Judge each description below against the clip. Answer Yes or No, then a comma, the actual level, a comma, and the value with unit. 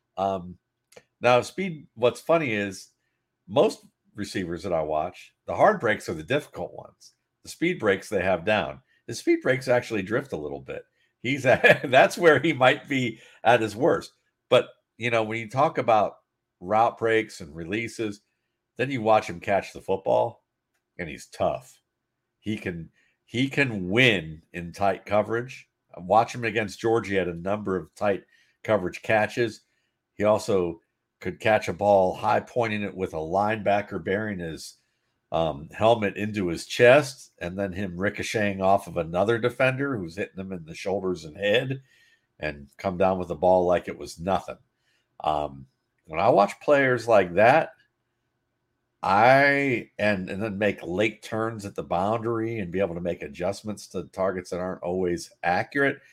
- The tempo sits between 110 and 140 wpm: No, average, 165 wpm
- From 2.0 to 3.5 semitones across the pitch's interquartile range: No, average, 4.4 semitones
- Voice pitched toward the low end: Yes, low, 105 Hz